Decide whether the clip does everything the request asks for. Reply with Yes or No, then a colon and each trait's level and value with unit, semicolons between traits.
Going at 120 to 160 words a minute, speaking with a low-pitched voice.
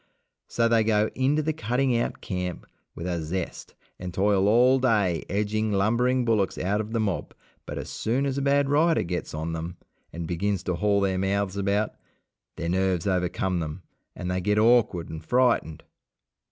No: average, 180 wpm; low, 100 Hz